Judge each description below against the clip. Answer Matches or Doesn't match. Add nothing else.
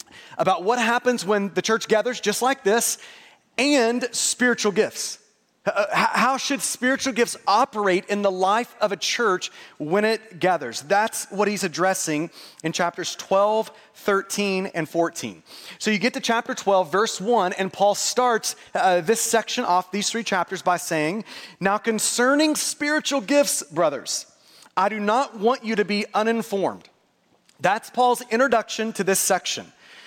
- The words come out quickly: Doesn't match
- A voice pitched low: Doesn't match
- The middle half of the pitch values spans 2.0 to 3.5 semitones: Doesn't match